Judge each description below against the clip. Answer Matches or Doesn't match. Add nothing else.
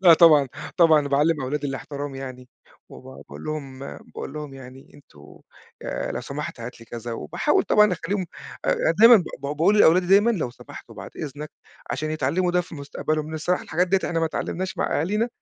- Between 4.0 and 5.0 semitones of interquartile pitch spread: Matches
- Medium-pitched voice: Matches